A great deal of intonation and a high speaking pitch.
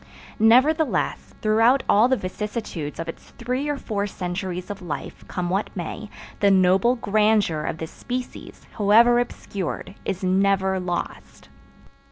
No: average, 4.3 semitones; high, 205 Hz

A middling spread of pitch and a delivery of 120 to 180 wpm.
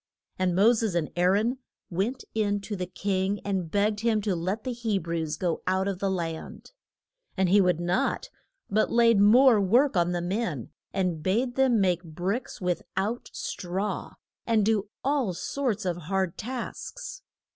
Yes: average, 4.1 semitones; average, 170 wpm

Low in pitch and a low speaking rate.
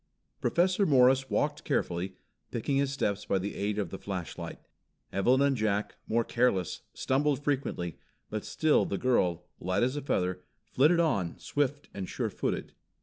No: low, 120 Hz; average, 155 wpm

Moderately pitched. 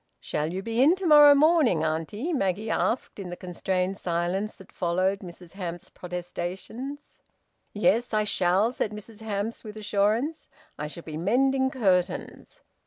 No: high, 200 Hz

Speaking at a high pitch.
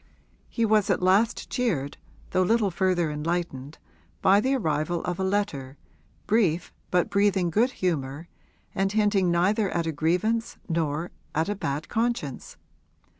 No: medium, 180 Hz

